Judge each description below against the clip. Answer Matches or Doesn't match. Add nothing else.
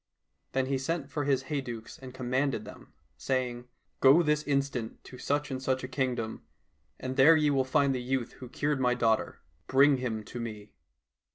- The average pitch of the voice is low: Matches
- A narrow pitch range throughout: Matches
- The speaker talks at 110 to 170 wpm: Doesn't match